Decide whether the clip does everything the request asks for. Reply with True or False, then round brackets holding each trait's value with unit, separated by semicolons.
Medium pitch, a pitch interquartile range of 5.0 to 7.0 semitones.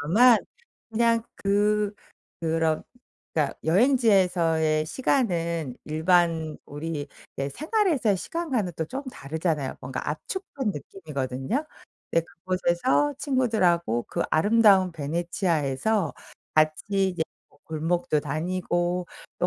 True (175 Hz; 5.5 semitones)